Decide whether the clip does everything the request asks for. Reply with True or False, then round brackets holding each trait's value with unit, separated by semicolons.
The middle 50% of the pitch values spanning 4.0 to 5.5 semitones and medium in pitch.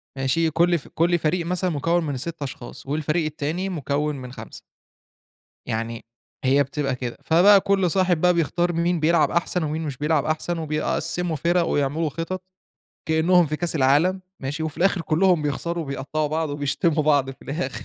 False (3.2 semitones; 160 Hz)